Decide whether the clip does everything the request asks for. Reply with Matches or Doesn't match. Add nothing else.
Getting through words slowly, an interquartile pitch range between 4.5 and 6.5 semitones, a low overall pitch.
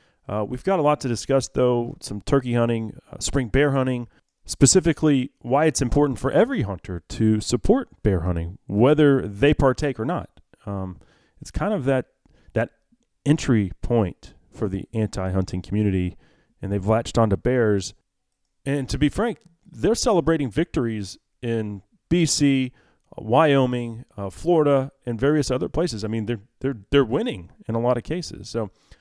Doesn't match